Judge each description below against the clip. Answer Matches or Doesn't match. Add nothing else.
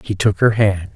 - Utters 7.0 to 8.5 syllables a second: Doesn't match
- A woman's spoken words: Doesn't match